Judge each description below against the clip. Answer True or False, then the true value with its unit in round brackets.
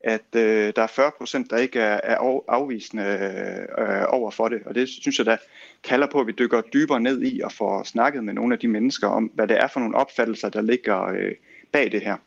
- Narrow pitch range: False (4.9 semitones)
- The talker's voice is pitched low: True (120 Hz)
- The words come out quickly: True (235 wpm)